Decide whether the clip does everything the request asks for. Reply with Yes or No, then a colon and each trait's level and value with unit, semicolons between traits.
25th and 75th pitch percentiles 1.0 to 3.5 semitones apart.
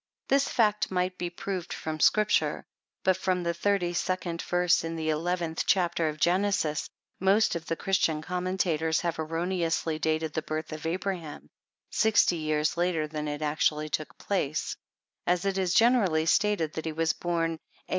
Yes: average, 2.8 semitones